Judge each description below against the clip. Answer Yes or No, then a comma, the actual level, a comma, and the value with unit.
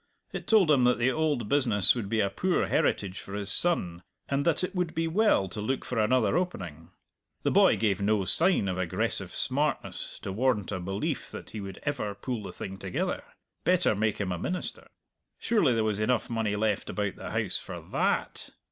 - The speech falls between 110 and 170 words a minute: No, average, 200 wpm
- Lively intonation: Yes, wide, 6.4 semitones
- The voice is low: Yes, low, 110 Hz